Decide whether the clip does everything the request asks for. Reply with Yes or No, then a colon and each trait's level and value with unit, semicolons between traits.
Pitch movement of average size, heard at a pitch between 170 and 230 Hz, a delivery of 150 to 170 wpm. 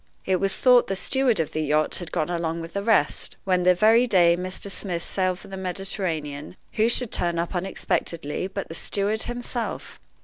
No: average, 3.3 semitones; medium, 185 Hz; average, 195 wpm